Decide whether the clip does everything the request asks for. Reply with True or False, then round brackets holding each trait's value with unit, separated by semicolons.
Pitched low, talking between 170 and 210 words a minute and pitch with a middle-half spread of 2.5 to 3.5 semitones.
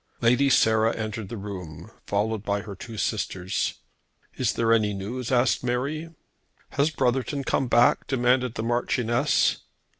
False (115 Hz; 140 wpm; 3.2 semitones)